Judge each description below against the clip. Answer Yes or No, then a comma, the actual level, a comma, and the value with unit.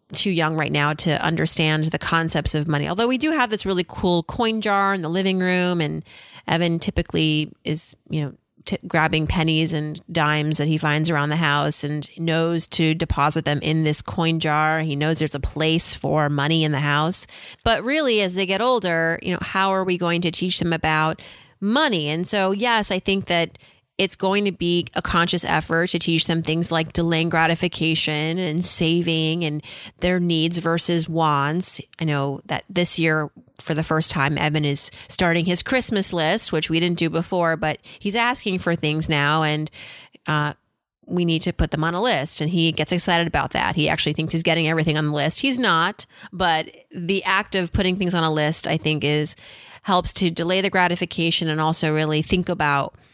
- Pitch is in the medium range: Yes, medium, 165 Hz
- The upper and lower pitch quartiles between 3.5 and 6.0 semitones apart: No, average, 2.7 semitones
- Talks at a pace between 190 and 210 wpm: Yes, average, 200 wpm